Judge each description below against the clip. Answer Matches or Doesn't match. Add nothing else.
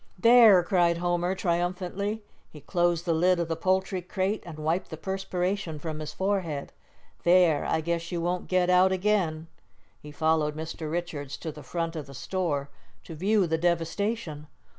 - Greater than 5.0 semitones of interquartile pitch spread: Doesn't match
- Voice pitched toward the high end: Doesn't match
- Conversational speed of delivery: Matches